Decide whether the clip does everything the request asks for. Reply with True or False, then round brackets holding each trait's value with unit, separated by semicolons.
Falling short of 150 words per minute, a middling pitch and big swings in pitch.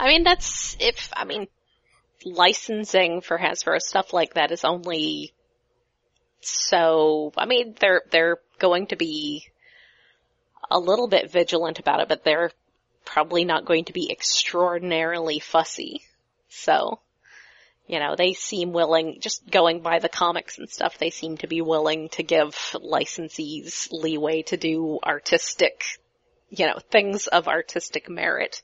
False (140 wpm; 170 Hz; 4.9 semitones)